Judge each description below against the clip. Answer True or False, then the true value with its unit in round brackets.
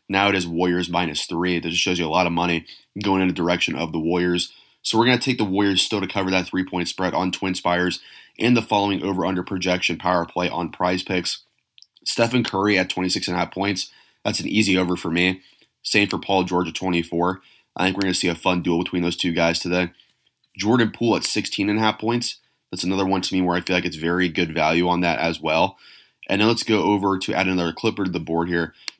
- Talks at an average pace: False (235 wpm)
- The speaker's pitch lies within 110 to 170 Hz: False (90 Hz)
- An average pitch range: False (1.8 semitones)